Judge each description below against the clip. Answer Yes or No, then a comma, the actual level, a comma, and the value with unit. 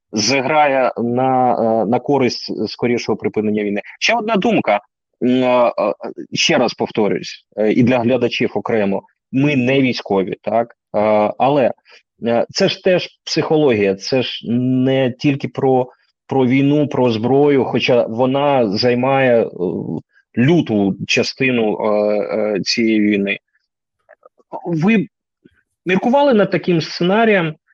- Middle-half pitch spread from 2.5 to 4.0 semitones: No, average, 4.4 semitones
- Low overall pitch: Yes, low, 130 Hz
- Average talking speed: No, slow, 100 wpm